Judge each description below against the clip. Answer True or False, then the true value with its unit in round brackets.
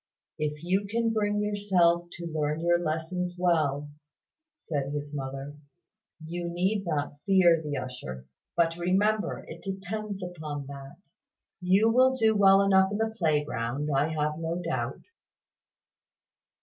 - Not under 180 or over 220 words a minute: False (135 wpm)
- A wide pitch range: False (4.8 semitones)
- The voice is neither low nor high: True (170 Hz)